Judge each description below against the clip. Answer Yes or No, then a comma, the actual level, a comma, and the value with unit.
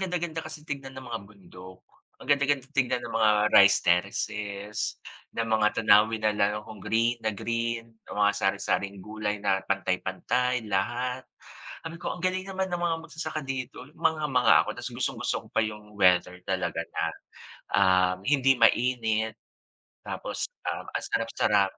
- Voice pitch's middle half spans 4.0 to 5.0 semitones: Yes, average, 4.7 semitones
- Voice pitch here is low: Yes, low, 115 Hz